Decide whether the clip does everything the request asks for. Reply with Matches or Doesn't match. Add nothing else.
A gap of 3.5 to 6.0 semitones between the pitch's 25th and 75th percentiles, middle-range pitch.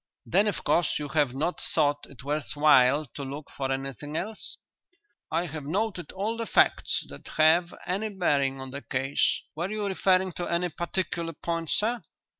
Matches